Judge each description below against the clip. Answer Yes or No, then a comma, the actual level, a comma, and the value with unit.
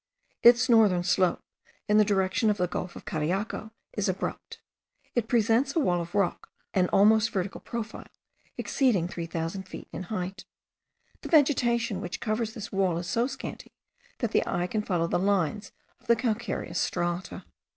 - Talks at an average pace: Yes, average, 160 wpm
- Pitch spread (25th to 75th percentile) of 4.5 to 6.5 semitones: No, average, 4.1 semitones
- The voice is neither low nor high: No, high, 200 Hz